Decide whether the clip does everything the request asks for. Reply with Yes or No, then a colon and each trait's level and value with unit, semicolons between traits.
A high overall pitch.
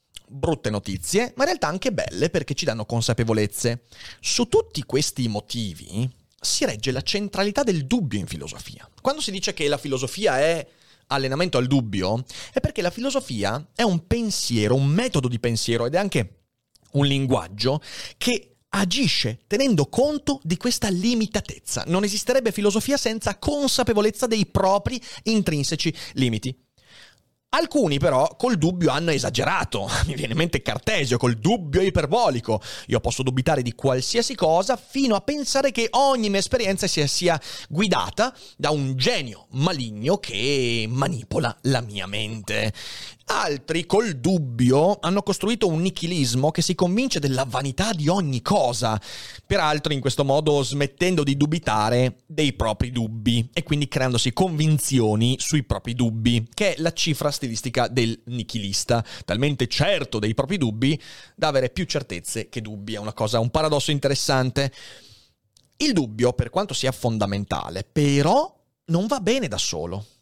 No: medium, 140 Hz